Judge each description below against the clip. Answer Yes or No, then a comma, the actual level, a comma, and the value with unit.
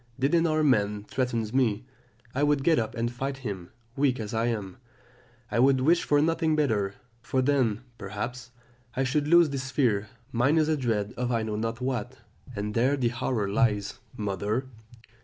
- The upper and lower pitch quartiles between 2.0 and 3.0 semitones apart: No, average, 4.4 semitones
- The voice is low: Yes, low, 125 Hz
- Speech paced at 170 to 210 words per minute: Yes, average, 180 wpm